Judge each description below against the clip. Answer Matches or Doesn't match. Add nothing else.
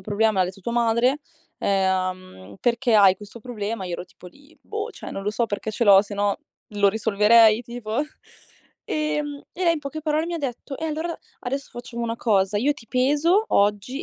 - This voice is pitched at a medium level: Doesn't match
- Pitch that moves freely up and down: Matches